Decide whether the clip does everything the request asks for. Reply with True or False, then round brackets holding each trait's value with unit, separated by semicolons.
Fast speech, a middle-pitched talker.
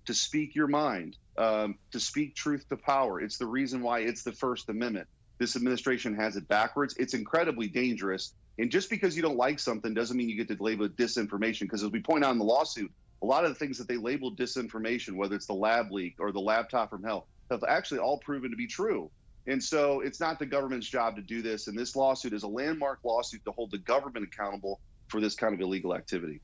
False (235 wpm; 120 Hz)